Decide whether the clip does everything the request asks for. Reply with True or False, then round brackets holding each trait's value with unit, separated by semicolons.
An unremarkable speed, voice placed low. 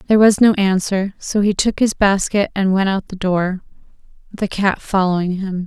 False (190 wpm; 195 Hz)